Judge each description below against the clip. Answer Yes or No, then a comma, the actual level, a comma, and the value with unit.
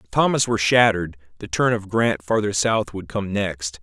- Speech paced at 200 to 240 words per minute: Yes, fast, 205 wpm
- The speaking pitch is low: Yes, low, 105 Hz